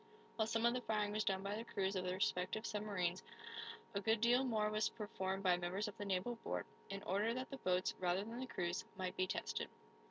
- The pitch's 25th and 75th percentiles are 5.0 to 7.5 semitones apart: No, average, 3.1 semitones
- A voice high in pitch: Yes, high, 205 Hz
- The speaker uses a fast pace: Yes, fast, 225 wpm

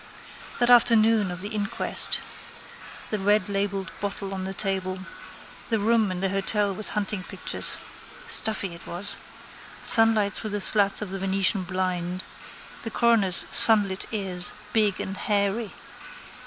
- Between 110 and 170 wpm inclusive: Yes, slow, 135 wpm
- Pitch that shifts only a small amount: Yes, narrow, 2.3 semitones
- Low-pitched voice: No, high, 200 Hz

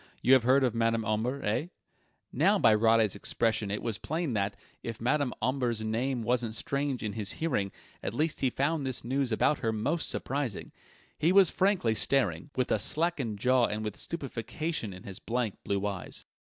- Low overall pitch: Yes, low, 120 Hz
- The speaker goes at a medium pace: Yes, average, 180 wpm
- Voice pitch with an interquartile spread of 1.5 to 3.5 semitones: No, average, 4.2 semitones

